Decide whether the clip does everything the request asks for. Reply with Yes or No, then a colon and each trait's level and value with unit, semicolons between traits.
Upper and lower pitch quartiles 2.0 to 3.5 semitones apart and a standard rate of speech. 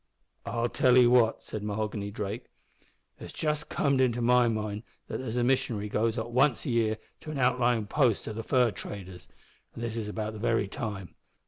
Yes: average, 2.8 semitones; average, 195 wpm